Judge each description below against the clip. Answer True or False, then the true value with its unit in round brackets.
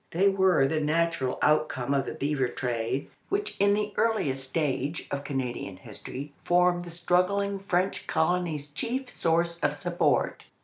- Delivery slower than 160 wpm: True (145 wpm)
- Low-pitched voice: False (165 Hz)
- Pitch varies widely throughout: False (4.8 semitones)